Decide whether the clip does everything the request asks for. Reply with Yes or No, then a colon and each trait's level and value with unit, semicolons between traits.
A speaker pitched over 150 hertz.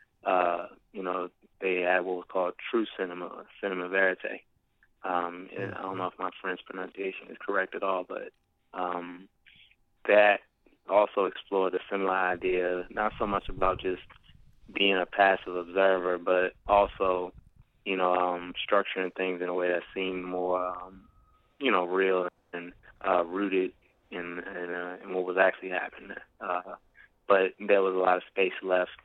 No: very low, 90 Hz